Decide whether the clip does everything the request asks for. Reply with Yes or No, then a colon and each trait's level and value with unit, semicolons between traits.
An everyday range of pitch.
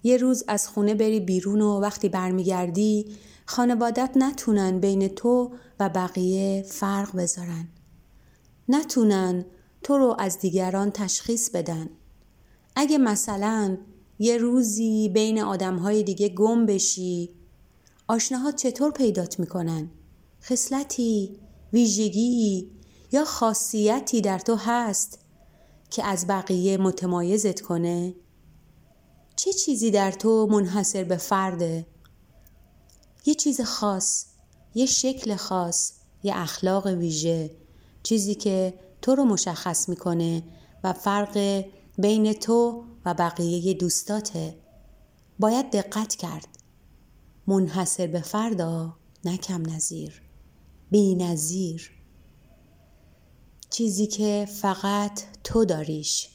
Yes: average, 3.6 semitones